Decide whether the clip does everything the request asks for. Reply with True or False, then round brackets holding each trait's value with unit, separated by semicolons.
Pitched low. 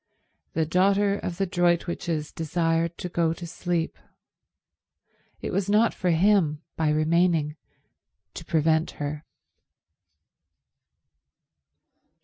False (170 Hz)